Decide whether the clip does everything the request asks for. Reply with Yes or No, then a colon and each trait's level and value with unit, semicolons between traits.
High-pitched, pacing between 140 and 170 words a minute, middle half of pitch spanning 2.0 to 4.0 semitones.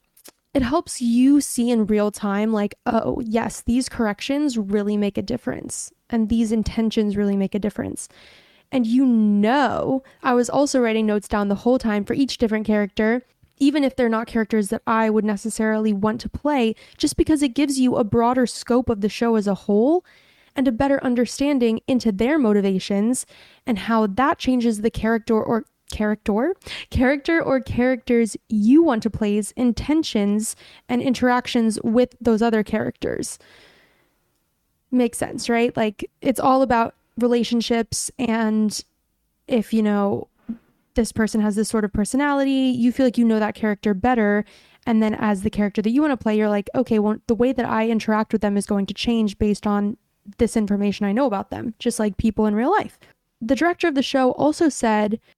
No: high, 230 Hz; average, 180 wpm; average, 3.0 semitones